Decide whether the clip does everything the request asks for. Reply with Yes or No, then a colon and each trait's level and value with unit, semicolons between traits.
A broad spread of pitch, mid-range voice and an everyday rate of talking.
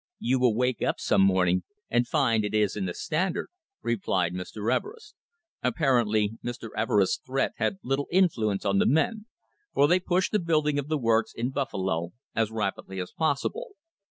No: wide, 6.5 semitones; low, 120 Hz; average, 170 wpm